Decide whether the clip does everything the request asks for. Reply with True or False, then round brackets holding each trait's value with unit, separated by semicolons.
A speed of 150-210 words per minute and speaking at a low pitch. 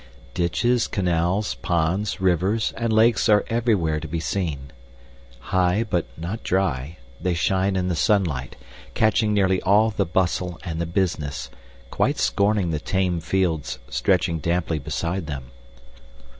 False (135 wpm; 90 Hz)